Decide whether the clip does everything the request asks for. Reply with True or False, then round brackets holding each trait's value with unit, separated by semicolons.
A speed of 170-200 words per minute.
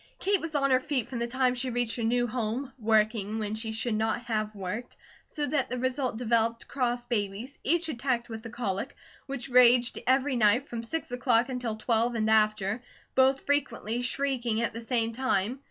True (190 wpm)